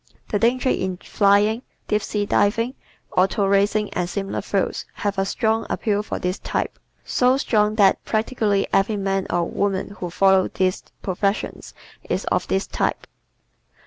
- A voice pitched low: No, high, 200 Hz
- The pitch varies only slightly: Yes, narrow, 2.0 semitones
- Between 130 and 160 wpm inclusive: Yes, average, 150 wpm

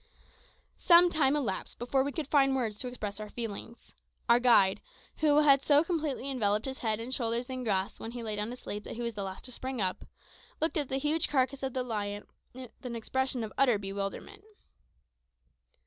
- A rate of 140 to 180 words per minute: No, average, 200 wpm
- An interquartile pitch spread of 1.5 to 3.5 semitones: No, average, 4.1 semitones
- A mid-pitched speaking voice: No, very high, 250 Hz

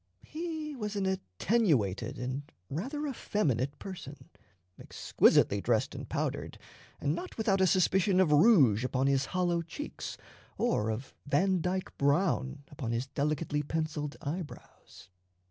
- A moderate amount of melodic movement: No, wide, 6.0 semitones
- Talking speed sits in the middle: No, slow, 125 wpm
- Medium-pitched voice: Yes, medium, 155 Hz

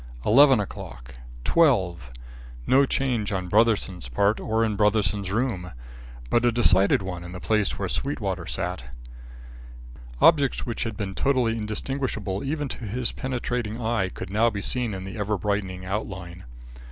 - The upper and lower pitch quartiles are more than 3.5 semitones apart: Yes, average, 4.1 semitones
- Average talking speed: Yes, average, 145 wpm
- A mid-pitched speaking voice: No, low, 105 Hz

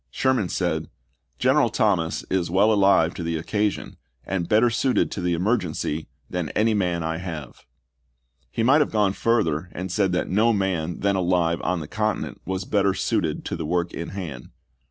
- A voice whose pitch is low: Yes, very low, 95 Hz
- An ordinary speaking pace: Yes, average, 180 wpm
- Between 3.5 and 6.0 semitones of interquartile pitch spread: Yes, average, 4.1 semitones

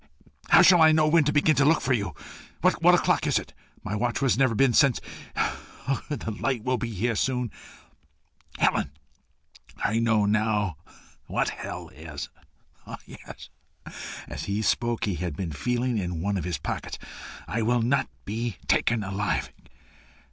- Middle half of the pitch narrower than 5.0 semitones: Yes, average, 4.3 semitones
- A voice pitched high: No, low, 115 Hz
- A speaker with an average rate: Yes, average, 160 wpm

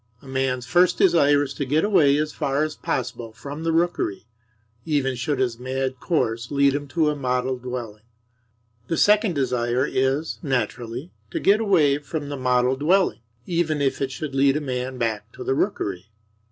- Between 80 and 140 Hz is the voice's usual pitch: Yes, low, 135 Hz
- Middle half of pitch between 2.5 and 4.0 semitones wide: Yes, average, 3.4 semitones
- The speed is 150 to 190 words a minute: Yes, average, 180 wpm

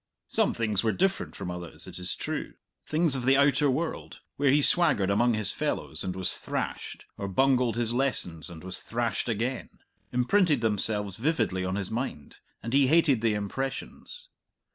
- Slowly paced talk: No, average, 170 wpm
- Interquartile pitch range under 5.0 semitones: No, wide, 5.5 semitones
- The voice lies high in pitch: No, low, 120 Hz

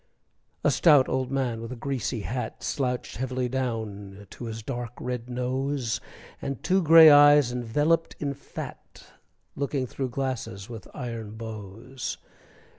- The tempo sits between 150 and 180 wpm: No, slow, 135 wpm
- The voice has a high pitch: No, low, 125 Hz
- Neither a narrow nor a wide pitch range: Yes, average, 3.2 semitones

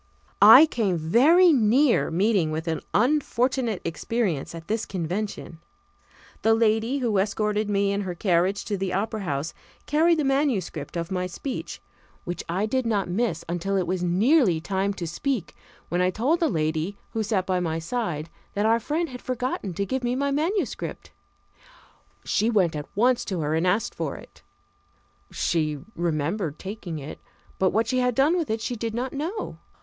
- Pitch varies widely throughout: Yes, wide, 6.0 semitones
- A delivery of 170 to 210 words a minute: Yes, average, 175 wpm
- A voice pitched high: Yes, high, 205 Hz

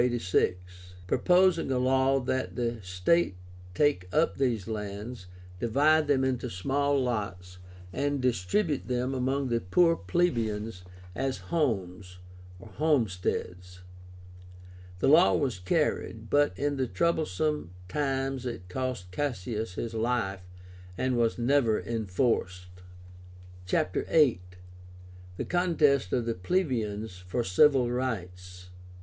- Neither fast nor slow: No, slow, 110 wpm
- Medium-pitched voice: No, low, 125 Hz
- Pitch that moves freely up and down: Yes, wide, 6.7 semitones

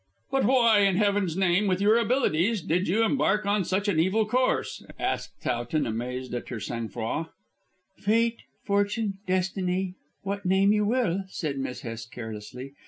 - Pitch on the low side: No, high, 190 Hz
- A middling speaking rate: Yes, average, 160 wpm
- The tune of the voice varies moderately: No, wide, 6.3 semitones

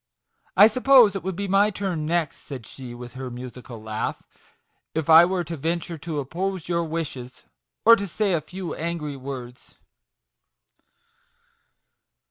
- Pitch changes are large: Yes, wide, 6.0 semitones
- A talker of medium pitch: Yes, medium, 165 Hz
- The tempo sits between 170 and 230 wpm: No, average, 150 wpm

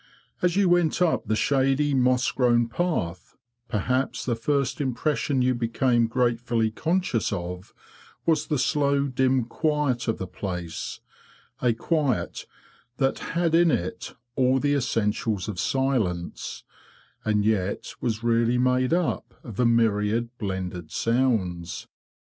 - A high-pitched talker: No, low, 125 Hz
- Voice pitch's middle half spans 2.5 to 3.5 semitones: No, average, 4.2 semitones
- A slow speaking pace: Yes, slow, 125 wpm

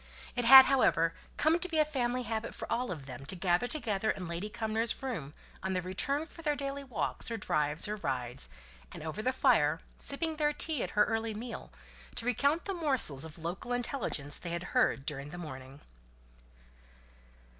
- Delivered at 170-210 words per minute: Yes, average, 190 wpm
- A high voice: Yes, high, 220 Hz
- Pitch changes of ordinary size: No, wide, 8.4 semitones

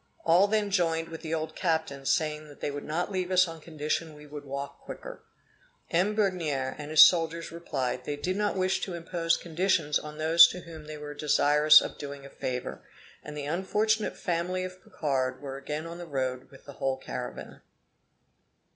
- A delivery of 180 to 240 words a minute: Yes, average, 185 wpm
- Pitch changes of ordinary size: Yes, average, 3.4 semitones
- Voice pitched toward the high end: No, medium, 160 Hz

